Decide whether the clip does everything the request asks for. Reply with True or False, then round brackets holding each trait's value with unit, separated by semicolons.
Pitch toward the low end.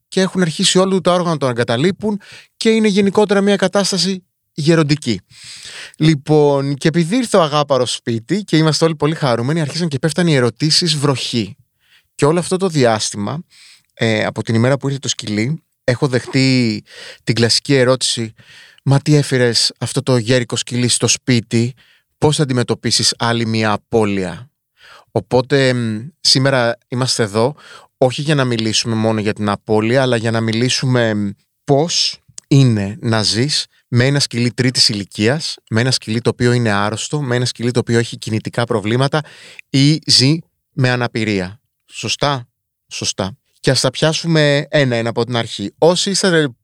True (130 Hz)